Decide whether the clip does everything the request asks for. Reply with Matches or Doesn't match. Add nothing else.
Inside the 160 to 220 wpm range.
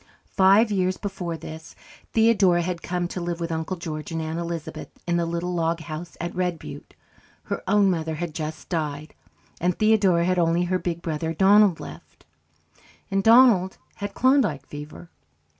Matches